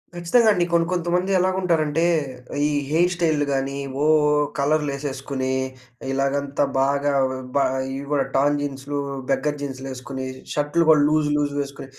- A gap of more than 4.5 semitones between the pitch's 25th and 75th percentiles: No, average, 2.9 semitones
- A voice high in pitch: No, medium, 145 Hz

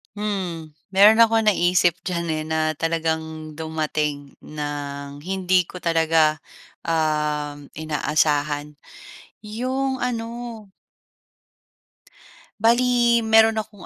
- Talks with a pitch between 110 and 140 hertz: No, medium, 165 Hz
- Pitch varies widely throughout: Yes, wide, 5.7 semitones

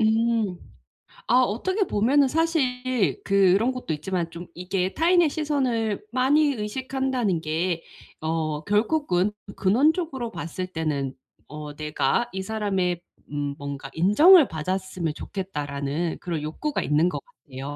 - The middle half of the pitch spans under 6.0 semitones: No, wide, 8.0 semitones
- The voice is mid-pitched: No, high, 195 Hz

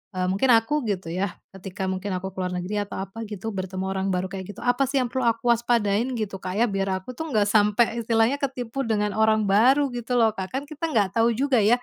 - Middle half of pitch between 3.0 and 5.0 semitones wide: Yes, average, 3.9 semitones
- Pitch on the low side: No, high, 215 Hz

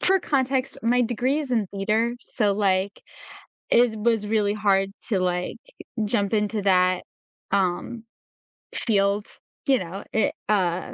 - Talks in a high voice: Yes, high, 210 Hz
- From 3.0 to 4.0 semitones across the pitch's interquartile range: Yes, average, 3.4 semitones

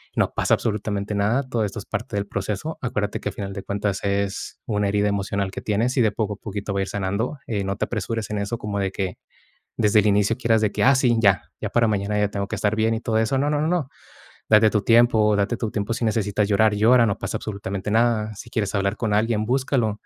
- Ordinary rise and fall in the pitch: No, narrow, 2.2 semitones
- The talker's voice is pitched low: Yes, low, 105 Hz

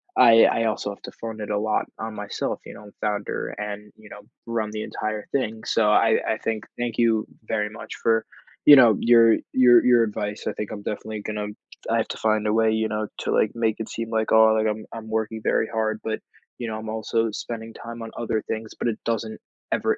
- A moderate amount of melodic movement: No, narrow, 1.1 semitones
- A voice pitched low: Yes, low, 110 Hz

